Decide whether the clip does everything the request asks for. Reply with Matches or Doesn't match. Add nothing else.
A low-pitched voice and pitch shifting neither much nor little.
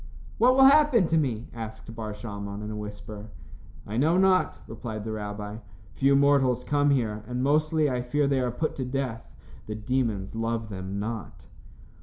Matches